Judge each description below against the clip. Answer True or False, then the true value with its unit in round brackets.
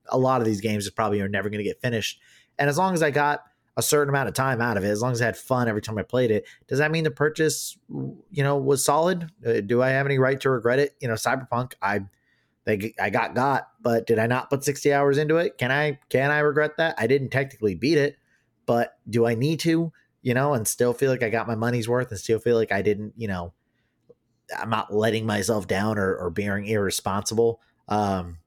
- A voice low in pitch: True (120 Hz)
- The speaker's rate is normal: False (245 wpm)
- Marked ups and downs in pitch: False (4.4 semitones)